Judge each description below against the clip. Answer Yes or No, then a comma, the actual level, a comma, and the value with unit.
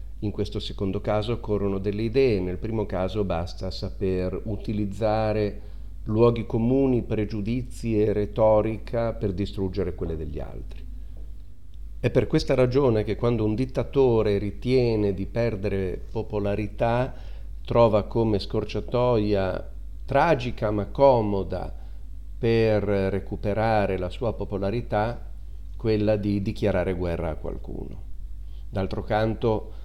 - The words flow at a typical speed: No, slow, 110 wpm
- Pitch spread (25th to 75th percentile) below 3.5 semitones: Yes, average, 2.9 semitones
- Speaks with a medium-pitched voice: No, low, 105 Hz